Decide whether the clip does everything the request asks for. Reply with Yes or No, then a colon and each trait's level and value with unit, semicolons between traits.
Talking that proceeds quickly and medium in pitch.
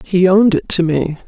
Yes: fast, 235 wpm; medium, 180 Hz